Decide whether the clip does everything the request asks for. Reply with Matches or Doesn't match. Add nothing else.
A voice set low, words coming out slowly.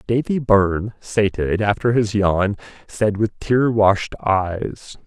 Matches